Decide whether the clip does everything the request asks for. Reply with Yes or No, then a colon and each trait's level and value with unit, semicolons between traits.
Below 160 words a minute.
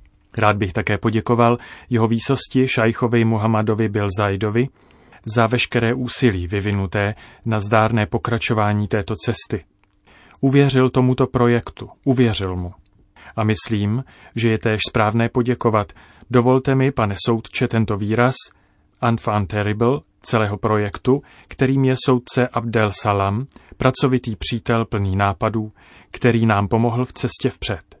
Yes: average, 120 wpm